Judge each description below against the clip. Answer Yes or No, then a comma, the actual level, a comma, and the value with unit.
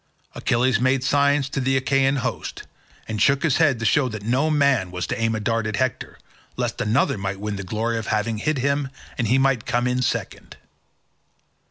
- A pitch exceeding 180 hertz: No, low, 125 Hz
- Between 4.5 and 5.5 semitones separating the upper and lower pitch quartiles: No, average, 3.9 semitones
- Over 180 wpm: Yes, fast, 205 wpm